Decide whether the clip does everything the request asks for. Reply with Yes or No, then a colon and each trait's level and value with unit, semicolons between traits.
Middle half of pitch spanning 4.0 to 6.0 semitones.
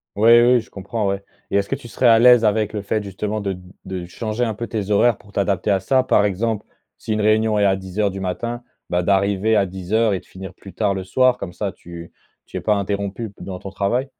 No: narrow, 2.4 semitones